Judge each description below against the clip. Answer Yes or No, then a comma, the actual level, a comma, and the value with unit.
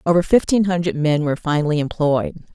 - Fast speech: No, average, 165 wpm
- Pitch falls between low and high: Yes, medium, 160 Hz